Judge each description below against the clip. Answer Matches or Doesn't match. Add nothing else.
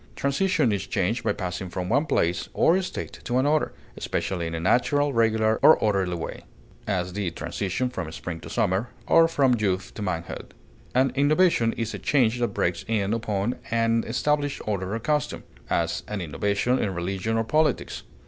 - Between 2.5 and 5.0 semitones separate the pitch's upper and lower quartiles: Doesn't match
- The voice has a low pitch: Matches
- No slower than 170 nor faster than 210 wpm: Matches